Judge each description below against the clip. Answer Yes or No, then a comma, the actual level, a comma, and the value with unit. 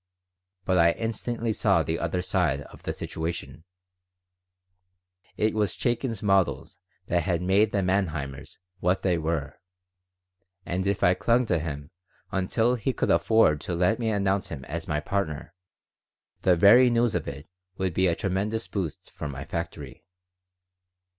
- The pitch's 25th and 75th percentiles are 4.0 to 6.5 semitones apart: Yes, average, 4.6 semitones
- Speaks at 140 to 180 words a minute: Yes, average, 150 wpm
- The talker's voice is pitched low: Yes, very low, 90 Hz